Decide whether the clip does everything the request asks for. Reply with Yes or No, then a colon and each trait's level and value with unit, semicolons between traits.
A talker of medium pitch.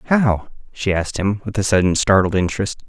No: low, 100 Hz